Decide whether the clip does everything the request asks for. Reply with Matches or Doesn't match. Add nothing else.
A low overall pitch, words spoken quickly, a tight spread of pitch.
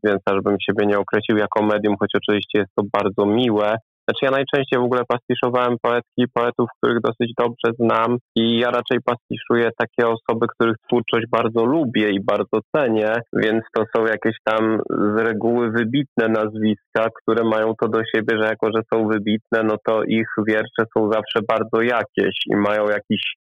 Matches